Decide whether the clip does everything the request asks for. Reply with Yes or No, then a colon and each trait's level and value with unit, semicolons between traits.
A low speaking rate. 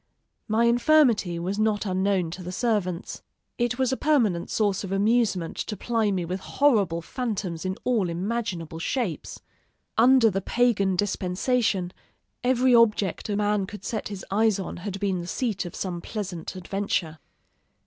No: average, 155 wpm